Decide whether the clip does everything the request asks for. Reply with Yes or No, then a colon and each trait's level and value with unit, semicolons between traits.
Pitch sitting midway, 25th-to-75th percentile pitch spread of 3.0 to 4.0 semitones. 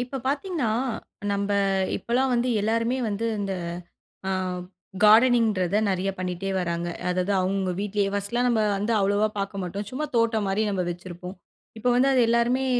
No: high, 205 Hz; average, 3.7 semitones